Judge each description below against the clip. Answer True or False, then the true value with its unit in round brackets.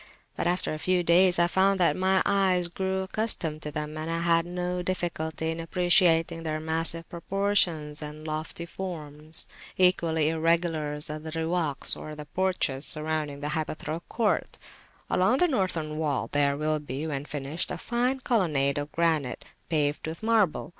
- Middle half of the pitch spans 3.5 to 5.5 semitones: False (3.0 semitones)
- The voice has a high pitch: False (165 Hz)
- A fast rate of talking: False (160 wpm)